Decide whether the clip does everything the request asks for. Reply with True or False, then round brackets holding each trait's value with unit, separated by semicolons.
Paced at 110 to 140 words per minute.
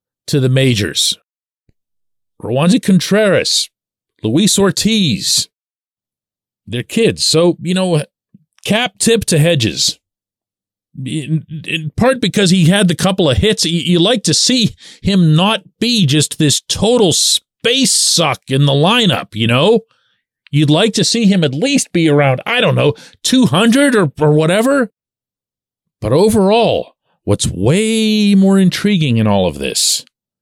True (135 wpm)